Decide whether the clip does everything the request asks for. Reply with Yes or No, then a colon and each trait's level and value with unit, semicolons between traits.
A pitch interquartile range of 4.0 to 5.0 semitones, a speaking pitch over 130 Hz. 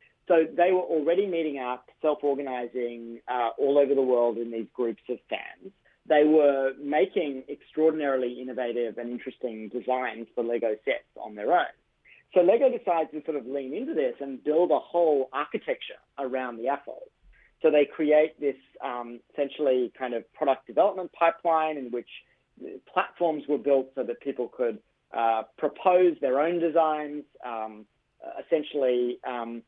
Yes: average, 4.6 semitones; medium, 140 Hz